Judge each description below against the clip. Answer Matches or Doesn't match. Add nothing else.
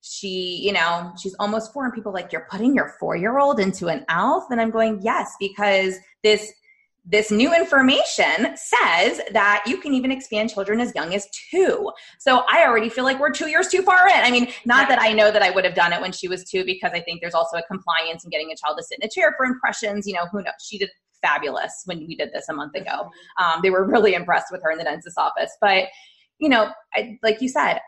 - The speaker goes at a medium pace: Doesn't match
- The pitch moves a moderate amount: Doesn't match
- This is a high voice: Matches